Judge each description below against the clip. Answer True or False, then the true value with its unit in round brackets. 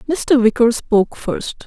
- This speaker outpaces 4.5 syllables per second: False (4.1 syllables/s)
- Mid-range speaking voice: False (250 Hz)